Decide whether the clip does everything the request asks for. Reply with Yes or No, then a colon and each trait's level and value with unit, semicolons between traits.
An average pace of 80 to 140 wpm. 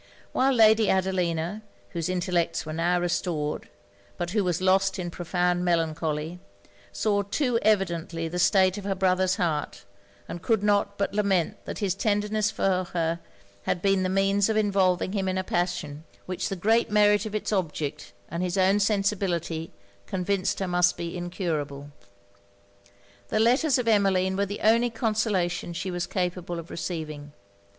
No: average, 160 wpm